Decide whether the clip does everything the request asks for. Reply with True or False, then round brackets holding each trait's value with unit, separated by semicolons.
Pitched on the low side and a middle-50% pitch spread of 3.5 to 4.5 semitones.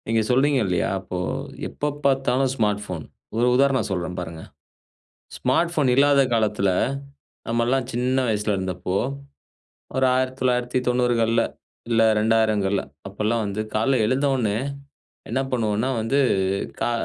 True (115 Hz; 3.8 semitones)